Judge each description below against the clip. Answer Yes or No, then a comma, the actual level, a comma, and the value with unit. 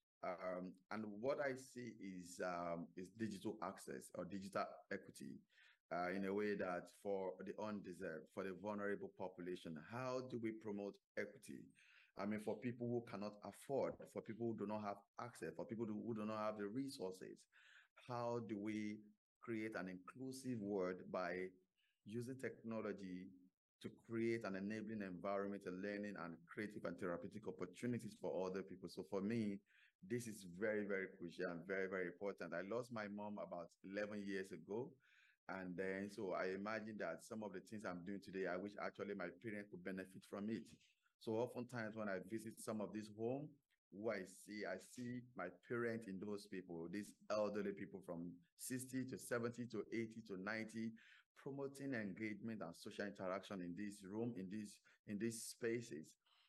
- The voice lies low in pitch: Yes, low, 105 Hz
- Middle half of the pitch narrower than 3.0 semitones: No, average, 3.3 semitones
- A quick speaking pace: No, average, 175 wpm